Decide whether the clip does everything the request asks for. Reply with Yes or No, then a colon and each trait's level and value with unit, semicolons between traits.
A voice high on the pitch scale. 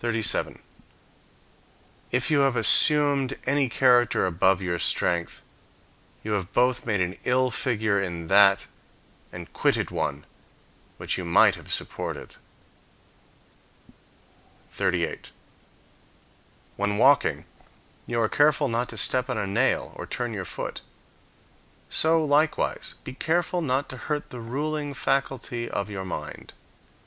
No: low, 120 Hz